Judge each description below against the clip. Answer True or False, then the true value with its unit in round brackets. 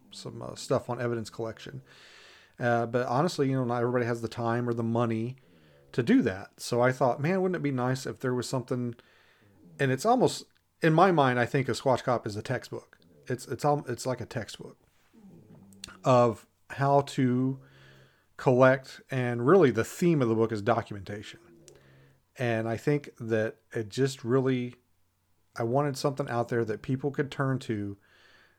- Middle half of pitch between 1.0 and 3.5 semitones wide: True (2.8 semitones)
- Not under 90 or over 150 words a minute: False (180 wpm)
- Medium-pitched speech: False (120 Hz)